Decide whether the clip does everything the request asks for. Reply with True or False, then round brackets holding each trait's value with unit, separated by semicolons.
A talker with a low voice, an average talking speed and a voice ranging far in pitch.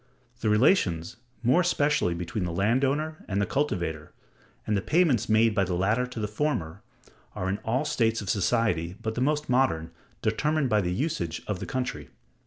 True (110 Hz; 185 wpm; 6.8 semitones)